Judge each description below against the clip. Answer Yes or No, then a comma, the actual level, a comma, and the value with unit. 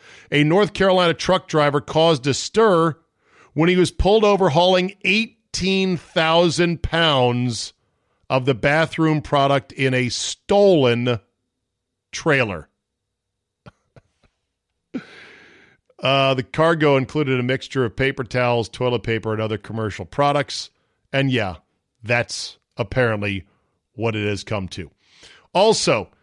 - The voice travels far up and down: Yes, wide, 6.3 semitones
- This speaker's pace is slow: Yes, slow, 110 wpm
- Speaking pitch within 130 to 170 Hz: Yes, low, 135 Hz